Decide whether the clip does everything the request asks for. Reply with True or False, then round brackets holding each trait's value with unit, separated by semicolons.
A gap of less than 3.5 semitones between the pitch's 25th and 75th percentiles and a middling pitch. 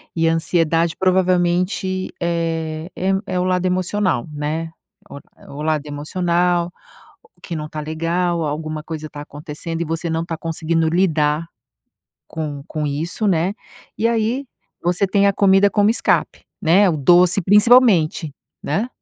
True (2.9 semitones; 170 Hz)